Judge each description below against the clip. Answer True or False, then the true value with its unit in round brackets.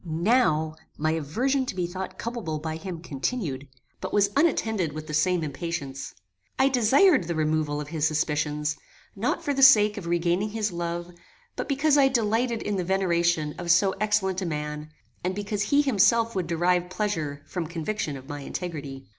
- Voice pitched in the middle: True (175 Hz)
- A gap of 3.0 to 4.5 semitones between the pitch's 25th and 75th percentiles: False (5.3 semitones)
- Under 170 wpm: False (175 wpm)